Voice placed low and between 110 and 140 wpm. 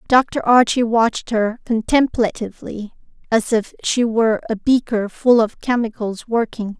No: high, 230 Hz; slow, 135 wpm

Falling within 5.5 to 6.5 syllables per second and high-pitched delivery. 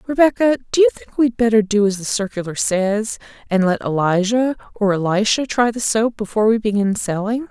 Yes: 5.6 syllables/s; high, 220 Hz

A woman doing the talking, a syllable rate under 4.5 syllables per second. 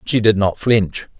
No: male; 4.0 syllables/s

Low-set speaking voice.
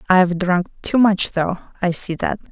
No: medium, 185 Hz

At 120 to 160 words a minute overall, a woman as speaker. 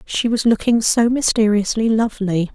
Yes: average, 140 wpm; female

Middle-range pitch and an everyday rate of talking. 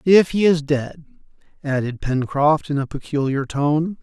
Yes: medium, 150 Hz; average, 150 wpm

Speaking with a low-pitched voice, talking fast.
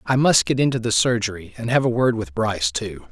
Yes: low, 115 Hz; fast, 230 wpm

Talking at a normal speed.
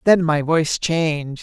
Yes: average, 170 wpm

